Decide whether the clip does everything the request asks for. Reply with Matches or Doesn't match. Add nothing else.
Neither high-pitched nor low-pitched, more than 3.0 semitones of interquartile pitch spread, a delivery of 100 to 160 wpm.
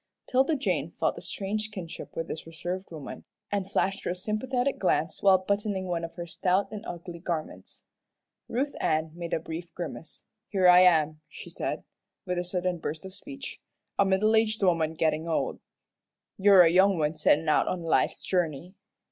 Doesn't match